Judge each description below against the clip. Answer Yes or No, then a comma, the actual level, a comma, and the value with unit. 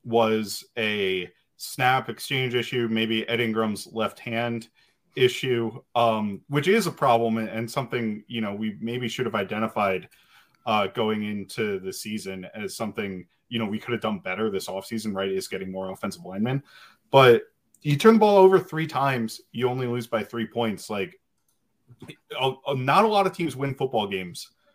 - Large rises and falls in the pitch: No, average, 3.6 semitones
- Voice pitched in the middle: No, low, 115 Hz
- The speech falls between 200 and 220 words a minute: No, average, 170 wpm